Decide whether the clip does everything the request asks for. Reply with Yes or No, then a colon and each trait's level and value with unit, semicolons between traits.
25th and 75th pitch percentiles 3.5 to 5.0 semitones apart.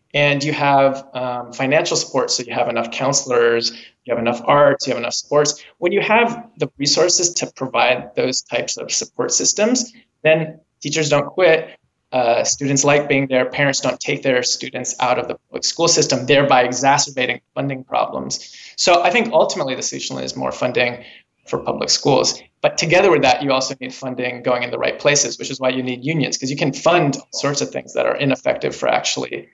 No: average, 3.0 semitones